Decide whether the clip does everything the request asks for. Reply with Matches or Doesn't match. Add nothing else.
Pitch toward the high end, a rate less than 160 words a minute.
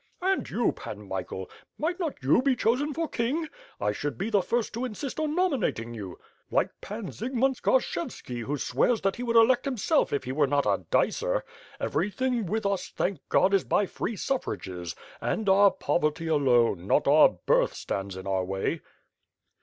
Doesn't match